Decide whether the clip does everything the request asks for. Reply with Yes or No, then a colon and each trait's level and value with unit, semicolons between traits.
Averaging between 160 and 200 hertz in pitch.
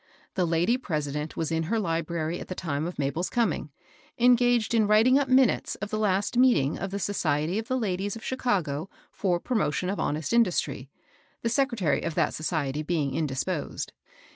Yes: medium, 185 Hz